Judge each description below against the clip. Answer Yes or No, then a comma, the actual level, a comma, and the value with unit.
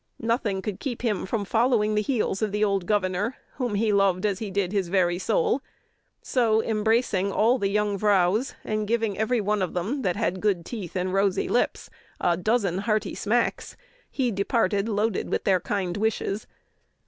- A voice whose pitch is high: Yes, high, 210 Hz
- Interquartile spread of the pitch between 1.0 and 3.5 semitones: Yes, average, 2.7 semitones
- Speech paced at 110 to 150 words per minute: No, average, 180 wpm